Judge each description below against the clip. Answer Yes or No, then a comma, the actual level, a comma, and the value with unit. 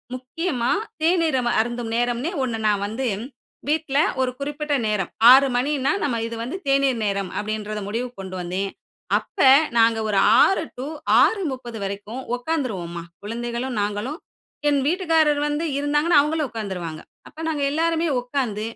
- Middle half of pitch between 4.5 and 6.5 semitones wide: Yes, wide, 5.5 semitones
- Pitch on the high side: Yes, very high, 250 Hz